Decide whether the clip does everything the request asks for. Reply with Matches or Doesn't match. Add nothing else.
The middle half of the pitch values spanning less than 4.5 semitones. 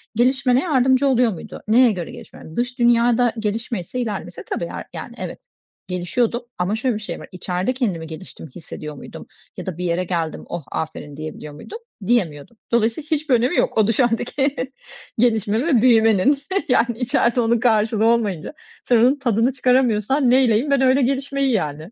Doesn't match